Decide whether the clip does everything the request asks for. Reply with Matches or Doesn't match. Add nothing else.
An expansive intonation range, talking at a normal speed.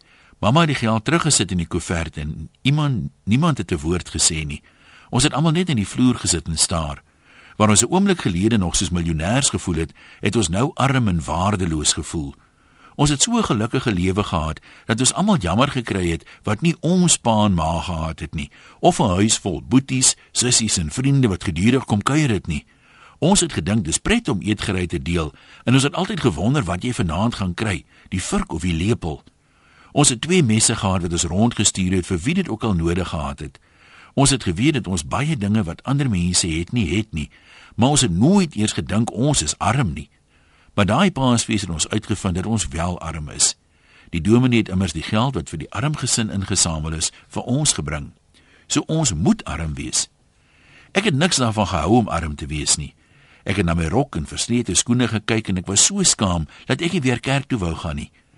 Doesn't match